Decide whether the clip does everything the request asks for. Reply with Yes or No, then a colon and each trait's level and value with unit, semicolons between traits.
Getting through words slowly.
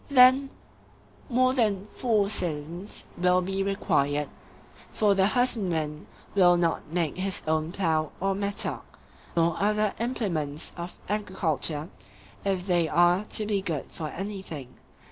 Yes: slow, 125 wpm